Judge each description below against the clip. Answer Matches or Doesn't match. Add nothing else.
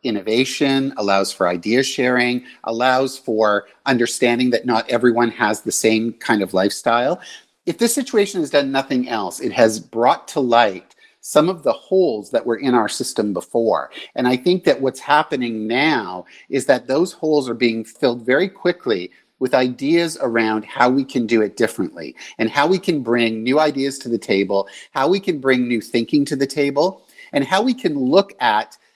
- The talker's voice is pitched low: Matches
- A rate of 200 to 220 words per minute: Doesn't match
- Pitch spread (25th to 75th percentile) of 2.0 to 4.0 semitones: Doesn't match